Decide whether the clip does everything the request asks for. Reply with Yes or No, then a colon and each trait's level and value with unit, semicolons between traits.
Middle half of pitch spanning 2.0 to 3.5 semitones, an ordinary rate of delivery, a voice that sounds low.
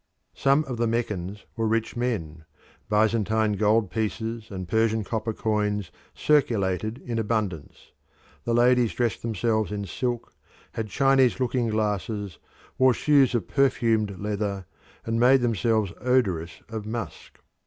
No: narrow, 2.4 semitones; slow, 130 wpm; low, 110 Hz